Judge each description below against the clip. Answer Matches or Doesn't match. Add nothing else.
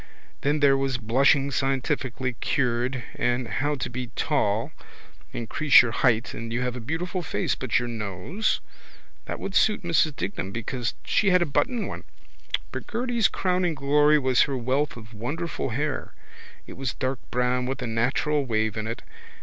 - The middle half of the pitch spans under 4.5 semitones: Matches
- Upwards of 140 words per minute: Matches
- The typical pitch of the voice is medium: Doesn't match